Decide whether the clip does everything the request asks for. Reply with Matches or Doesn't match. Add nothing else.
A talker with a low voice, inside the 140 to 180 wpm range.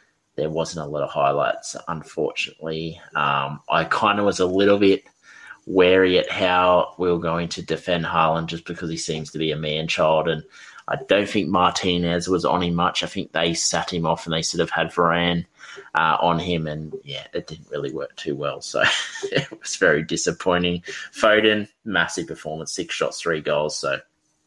Doesn't match